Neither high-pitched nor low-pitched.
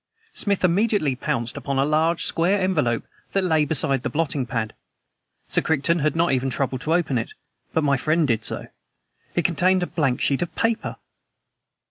Yes: medium, 155 Hz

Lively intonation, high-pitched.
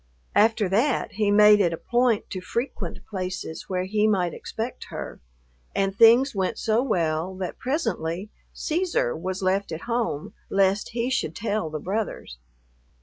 No: average, 3.9 semitones; high, 205 Hz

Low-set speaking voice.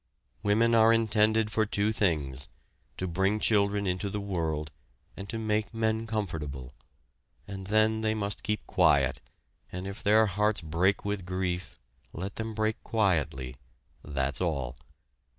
Yes: low, 100 Hz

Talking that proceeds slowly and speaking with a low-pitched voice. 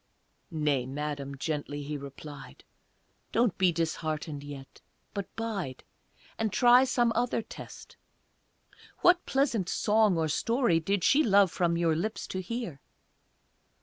No: slow, 125 wpm; medium, 170 Hz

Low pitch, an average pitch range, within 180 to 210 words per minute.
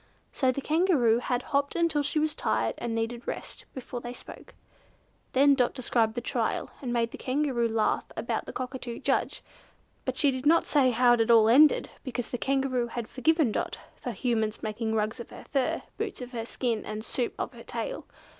No: high, 245 Hz; average, 3.2 semitones; average, 200 wpm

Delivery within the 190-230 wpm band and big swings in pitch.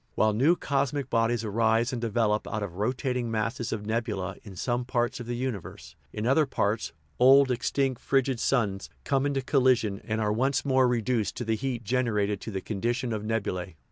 No: average, 195 wpm; average, 3.3 semitones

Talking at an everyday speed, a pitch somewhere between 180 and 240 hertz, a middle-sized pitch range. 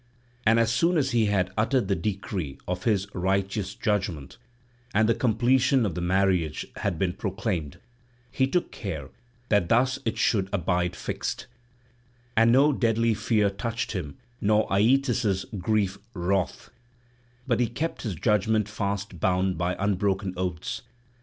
No: average, 145 wpm; low, 100 Hz; average, 3.7 semitones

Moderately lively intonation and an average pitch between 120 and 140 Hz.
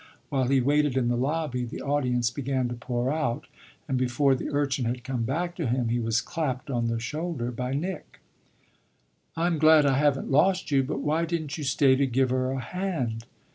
Yes: average, 3.3 semitones; low, 135 Hz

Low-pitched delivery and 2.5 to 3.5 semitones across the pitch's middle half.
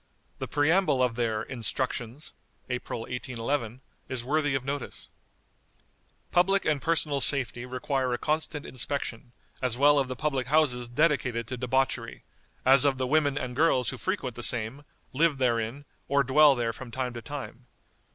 Yes: low, 130 Hz; average, 3.1 semitones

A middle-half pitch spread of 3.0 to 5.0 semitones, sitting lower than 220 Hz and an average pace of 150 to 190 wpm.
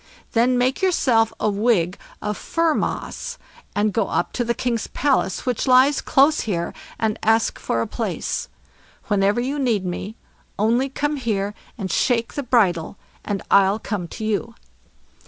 No: average, 4.1 semitones; high, 225 Hz; average, 155 wpm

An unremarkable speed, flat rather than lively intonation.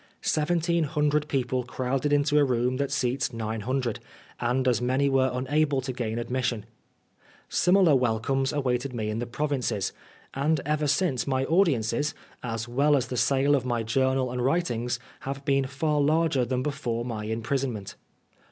No: average, 165 wpm; average, 3.0 semitones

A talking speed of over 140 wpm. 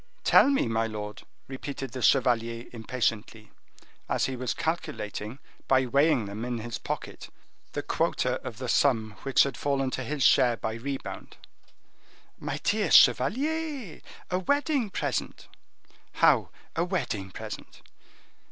No: slow, 135 wpm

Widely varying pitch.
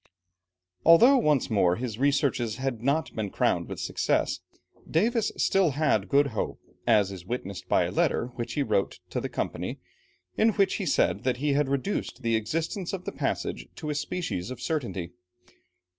Yes: wide, 6.4 semitones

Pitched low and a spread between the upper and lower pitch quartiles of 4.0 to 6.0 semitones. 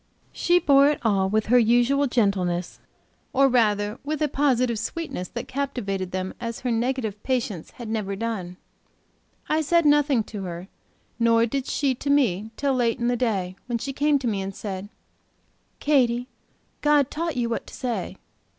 No: high, 235 Hz; average, 5.0 semitones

